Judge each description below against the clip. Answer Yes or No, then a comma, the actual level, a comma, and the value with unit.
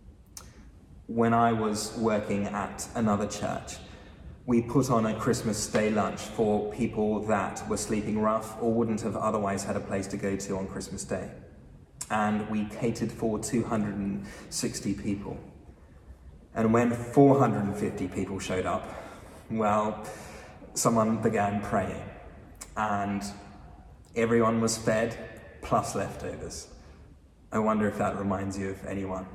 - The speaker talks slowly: Yes, slow, 130 wpm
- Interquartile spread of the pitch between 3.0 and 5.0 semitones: No, narrow, 2.4 semitones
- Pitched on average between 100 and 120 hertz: Yes, low, 105 Hz